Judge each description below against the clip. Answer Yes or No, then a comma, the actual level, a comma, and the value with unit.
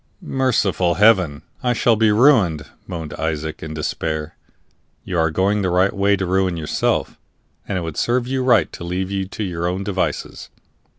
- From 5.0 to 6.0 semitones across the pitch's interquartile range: No, average, 4.2 semitones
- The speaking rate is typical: Yes, average, 175 wpm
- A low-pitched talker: Yes, very low, 95 Hz